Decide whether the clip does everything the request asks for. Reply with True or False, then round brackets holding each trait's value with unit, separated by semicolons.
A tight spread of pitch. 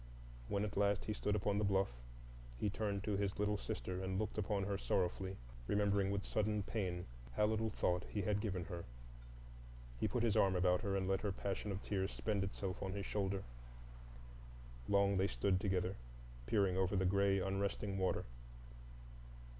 True (1.4 semitones)